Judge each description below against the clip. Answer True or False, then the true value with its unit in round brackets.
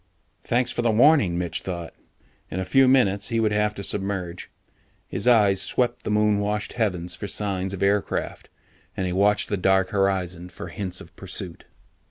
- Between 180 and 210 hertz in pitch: False (100 Hz)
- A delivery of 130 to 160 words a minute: False (180 wpm)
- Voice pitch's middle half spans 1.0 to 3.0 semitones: True (2.4 semitones)